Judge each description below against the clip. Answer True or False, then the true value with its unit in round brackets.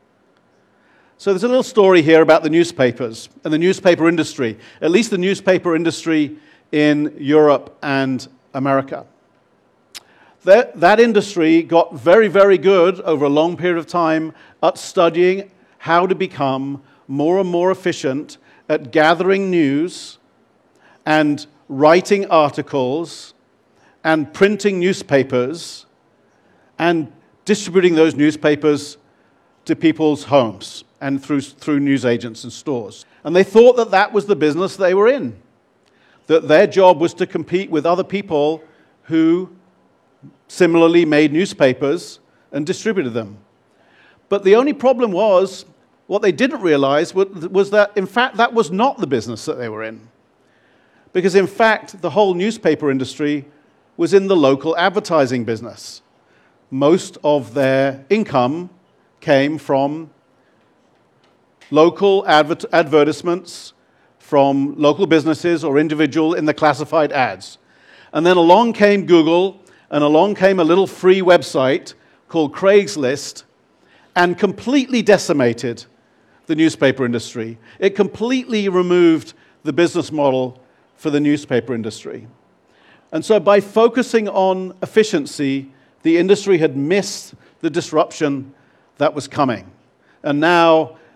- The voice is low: False (160 Hz)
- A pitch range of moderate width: True (4.9 semitones)